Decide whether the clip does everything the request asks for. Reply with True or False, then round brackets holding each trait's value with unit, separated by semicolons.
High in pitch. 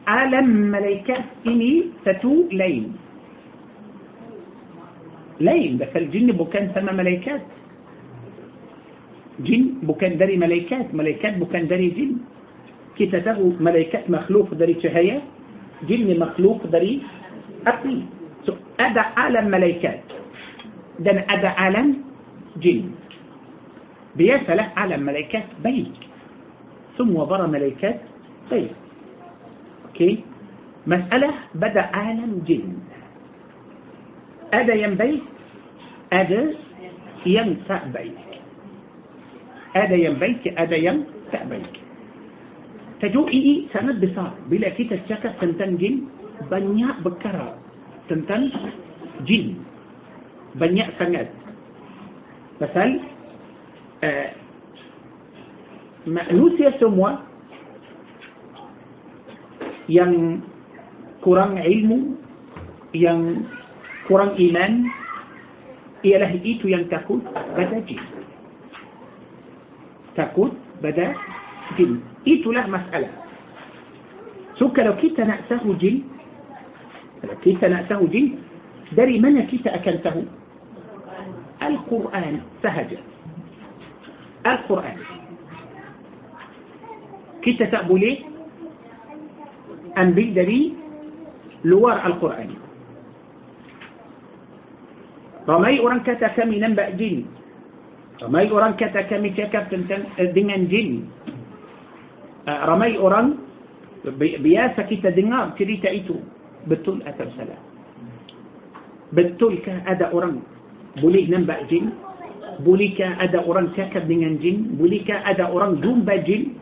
True (205 Hz)